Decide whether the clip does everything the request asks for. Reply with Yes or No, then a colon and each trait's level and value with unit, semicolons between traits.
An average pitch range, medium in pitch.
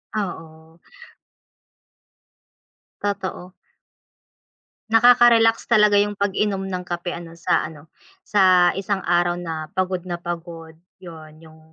Yes: average, 3.5 semitones; medium, 180 Hz